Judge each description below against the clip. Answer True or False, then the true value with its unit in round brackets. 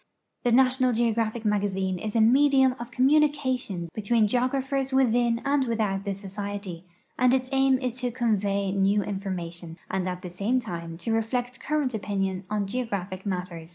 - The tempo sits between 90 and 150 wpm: False (160 wpm)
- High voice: True (220 Hz)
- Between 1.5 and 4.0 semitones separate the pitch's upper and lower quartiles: False (4.7 semitones)